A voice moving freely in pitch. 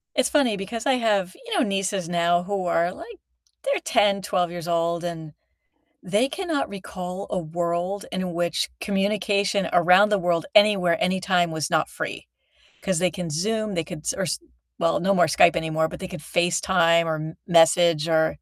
No: average, 2.9 semitones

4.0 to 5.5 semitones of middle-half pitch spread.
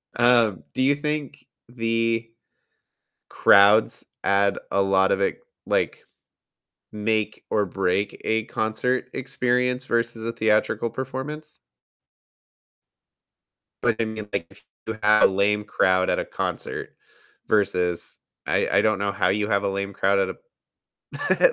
No: average, 3.5 semitones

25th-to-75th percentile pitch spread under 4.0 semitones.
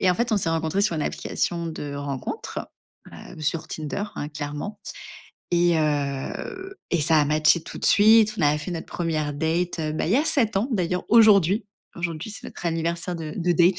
No: average, 4.4 semitones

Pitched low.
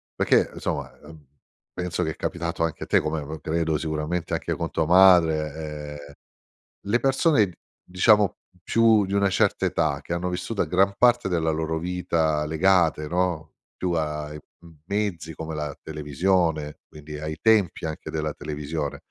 Yes: very low, 80 Hz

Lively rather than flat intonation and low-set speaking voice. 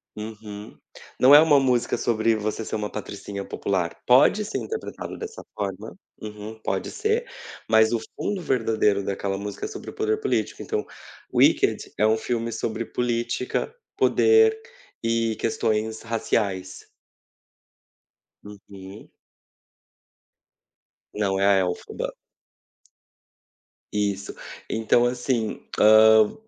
No: average, 3.3 semitones; low, 110 Hz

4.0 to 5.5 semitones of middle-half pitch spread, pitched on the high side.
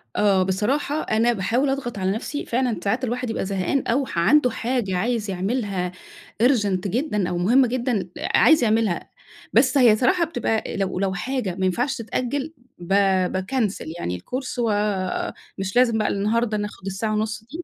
Yes: average, 4.5 semitones; high, 220 Hz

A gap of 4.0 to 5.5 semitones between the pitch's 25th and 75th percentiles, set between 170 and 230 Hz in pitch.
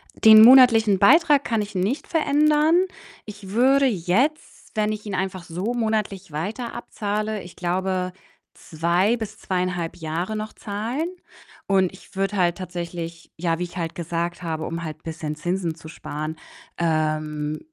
Yes: average, 4.5 semitones; high, 190 Hz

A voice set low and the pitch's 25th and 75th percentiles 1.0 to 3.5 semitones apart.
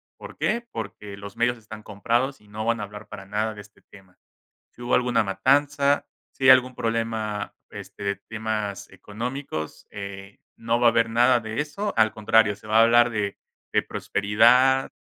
Yes: low, 110 Hz; average, 2.9 semitones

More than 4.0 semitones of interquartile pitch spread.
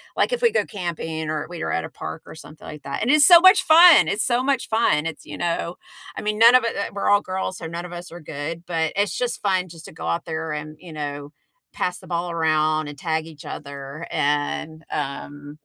Yes: average, 4.9 semitones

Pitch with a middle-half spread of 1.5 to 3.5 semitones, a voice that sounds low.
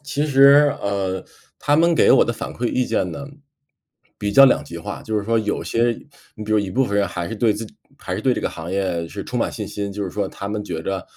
No: average, 4.2 semitones; low, 105 Hz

